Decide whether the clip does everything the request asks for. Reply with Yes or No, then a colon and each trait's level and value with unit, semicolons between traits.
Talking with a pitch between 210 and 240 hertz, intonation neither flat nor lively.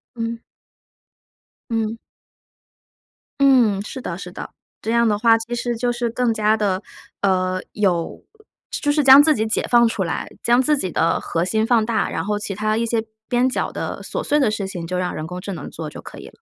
Yes: high, 220 Hz; average, 4.0 semitones